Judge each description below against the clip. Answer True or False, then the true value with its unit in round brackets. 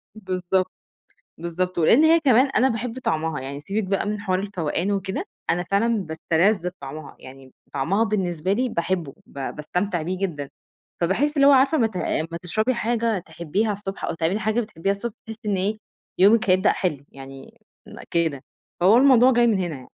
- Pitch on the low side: False (190 Hz)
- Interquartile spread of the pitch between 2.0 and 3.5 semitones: False (4.9 semitones)